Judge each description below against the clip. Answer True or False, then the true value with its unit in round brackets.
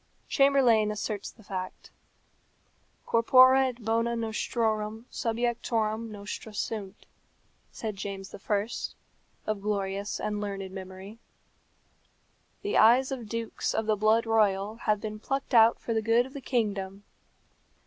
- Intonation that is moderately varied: False (2.2 semitones)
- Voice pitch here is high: True (220 Hz)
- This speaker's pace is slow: True (125 wpm)